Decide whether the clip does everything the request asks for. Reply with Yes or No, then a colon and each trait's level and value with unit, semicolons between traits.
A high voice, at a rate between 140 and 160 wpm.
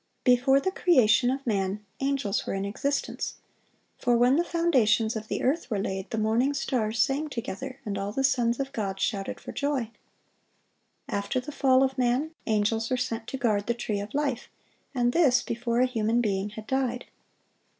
No: high, 240 Hz; average, 180 wpm